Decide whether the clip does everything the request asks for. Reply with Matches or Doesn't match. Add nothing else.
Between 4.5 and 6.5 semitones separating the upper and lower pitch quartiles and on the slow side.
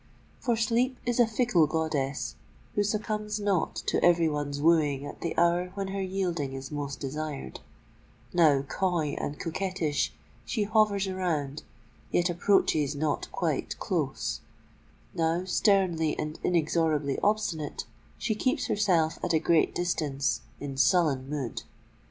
Matches